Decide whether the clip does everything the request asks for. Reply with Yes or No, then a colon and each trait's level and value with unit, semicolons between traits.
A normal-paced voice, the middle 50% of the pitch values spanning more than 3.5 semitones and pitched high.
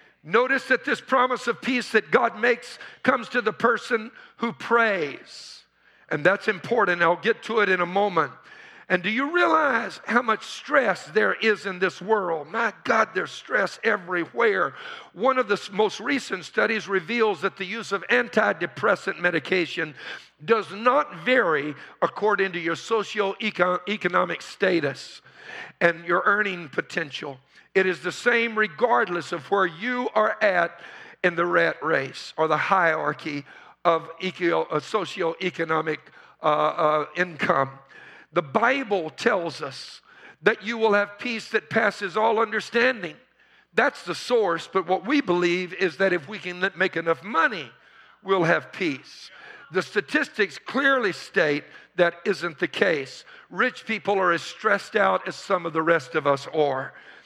Yes: average, 150 wpm; average, 4.9 semitones; high, 200 Hz